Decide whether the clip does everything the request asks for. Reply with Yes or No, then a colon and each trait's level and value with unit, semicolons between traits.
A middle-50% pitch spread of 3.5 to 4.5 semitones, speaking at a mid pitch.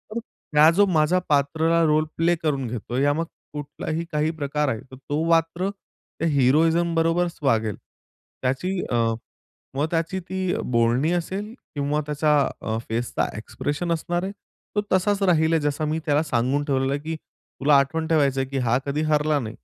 No: average, 3.0 semitones; medium, 150 Hz